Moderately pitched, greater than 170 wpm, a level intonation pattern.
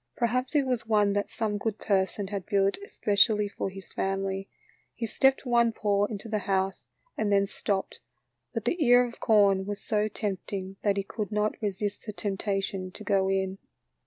No: high, 205 Hz; average, 180 wpm; narrow, 2.1 semitones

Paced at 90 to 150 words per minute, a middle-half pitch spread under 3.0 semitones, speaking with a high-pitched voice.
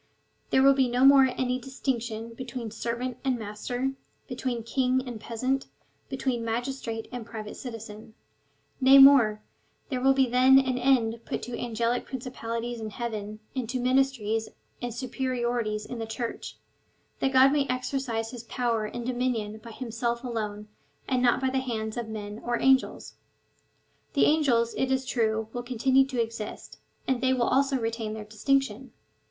No: average, 165 wpm; narrow, 2.6 semitones; high, 245 Hz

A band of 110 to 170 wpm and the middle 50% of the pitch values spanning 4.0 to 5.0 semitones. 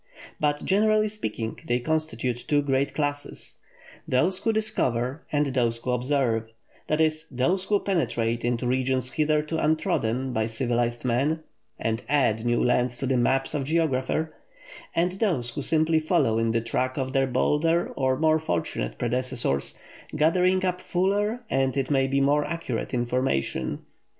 Yes: average, 155 wpm; average, 4.6 semitones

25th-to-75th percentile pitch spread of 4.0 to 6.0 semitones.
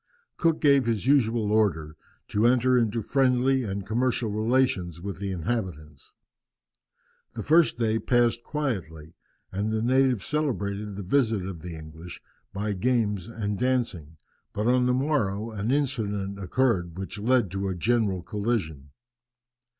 Yes: average, 4.6 semitones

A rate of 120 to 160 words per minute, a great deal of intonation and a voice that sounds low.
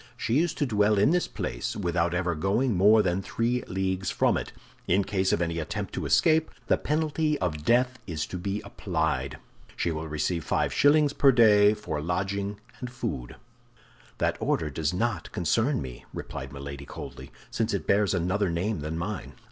No: average, 180 wpm; wide, 5.7 semitones; very low, 95 Hz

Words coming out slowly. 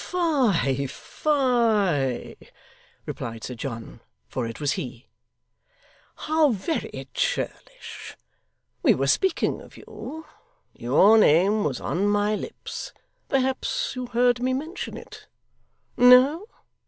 Yes: slow, 105 wpm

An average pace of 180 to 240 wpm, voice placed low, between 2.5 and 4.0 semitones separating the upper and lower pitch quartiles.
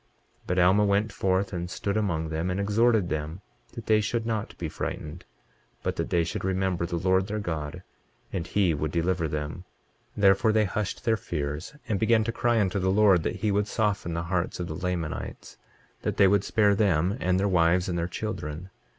Yes: fast, 205 wpm; very low, 95 Hz; average, 3.3 semitones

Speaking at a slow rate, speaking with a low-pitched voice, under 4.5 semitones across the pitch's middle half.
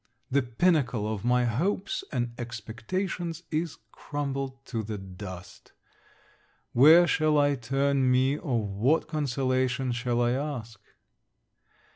Yes: slow, 115 wpm; low, 130 Hz; average, 3.6 semitones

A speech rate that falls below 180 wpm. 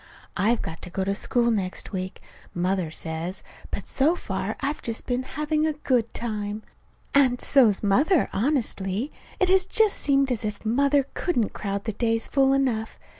Yes: average, 170 wpm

